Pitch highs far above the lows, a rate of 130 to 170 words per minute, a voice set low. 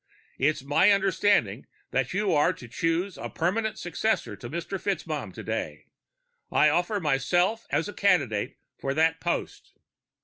No: wide, 5.7 semitones; average, 140 wpm; medium, 165 Hz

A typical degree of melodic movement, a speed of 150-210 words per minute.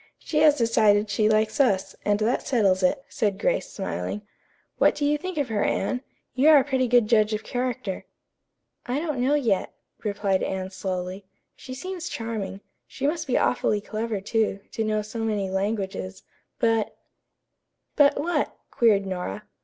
Yes: average, 4.6 semitones; average, 170 wpm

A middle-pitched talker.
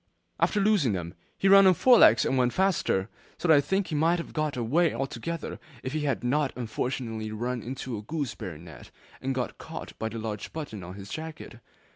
No: low, 130 Hz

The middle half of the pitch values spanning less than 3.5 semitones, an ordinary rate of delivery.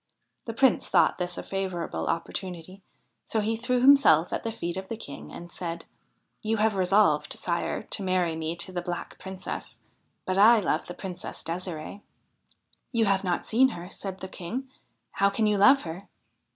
No: average, 3.9 semitones; average, 190 wpm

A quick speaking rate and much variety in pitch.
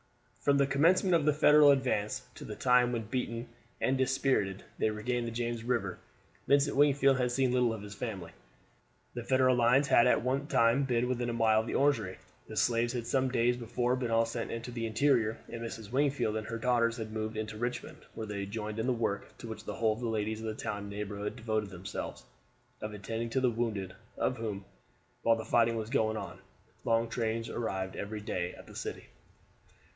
No: fast, 210 wpm; narrow, 2.5 semitones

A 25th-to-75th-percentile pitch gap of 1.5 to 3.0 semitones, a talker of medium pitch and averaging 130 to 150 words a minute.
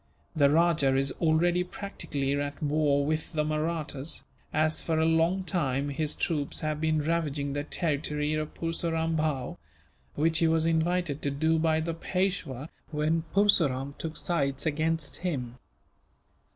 Yes: narrow, 2.4 semitones; medium, 155 Hz; average, 145 wpm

